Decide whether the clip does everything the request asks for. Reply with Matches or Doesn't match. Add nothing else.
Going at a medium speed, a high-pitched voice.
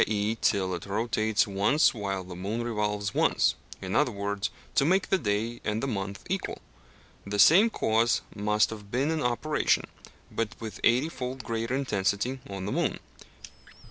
Doesn't match